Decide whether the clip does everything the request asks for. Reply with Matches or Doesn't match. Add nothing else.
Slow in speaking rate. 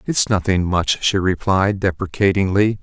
Matches